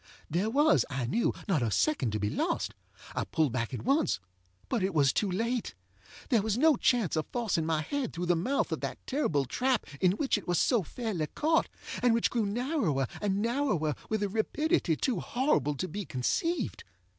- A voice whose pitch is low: No, high, 205 Hz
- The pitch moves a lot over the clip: Yes, wide, 8.3 semitones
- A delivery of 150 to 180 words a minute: No, average, 190 wpm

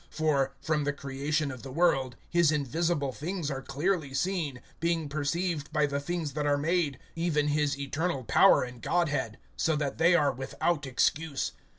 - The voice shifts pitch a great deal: No, average, 3.1 semitones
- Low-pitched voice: No, medium, 150 Hz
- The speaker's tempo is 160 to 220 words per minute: Yes, average, 170 wpm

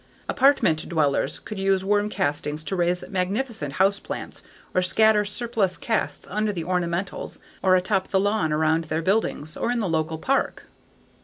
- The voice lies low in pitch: No, high, 190 Hz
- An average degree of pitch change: Yes, average, 4.5 semitones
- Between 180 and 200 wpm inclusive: No, average, 160 wpm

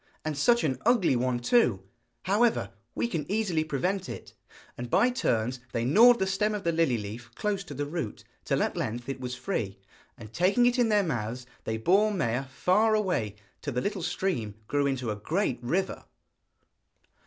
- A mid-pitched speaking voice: Yes, medium, 155 Hz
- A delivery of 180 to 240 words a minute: Yes, average, 185 wpm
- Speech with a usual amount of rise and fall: No, wide, 8.8 semitones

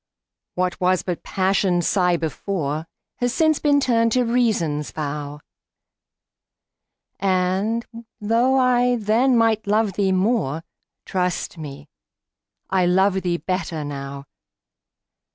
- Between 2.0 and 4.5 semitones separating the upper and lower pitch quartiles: No, wide, 5.4 semitones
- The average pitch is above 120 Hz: Yes, high, 190 Hz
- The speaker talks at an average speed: No, slow, 110 wpm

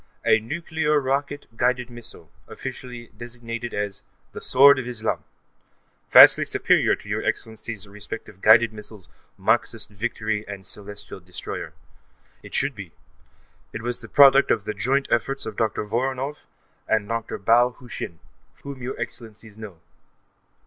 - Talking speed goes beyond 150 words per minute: No, average, 140 wpm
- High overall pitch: No, low, 115 Hz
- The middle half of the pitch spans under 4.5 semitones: Yes, average, 3.1 semitones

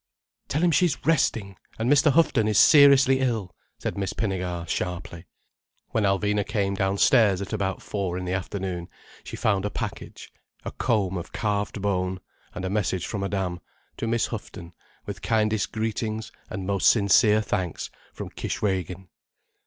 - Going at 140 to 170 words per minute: Yes, average, 155 wpm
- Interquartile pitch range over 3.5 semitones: No, average, 3.0 semitones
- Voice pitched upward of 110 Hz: No, low, 100 Hz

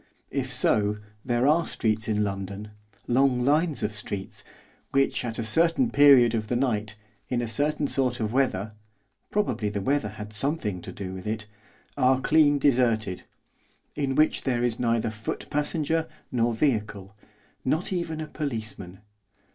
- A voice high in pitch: No, low, 120 Hz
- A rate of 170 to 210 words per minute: No, average, 155 wpm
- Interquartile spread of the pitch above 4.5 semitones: Yes, average, 5.1 semitones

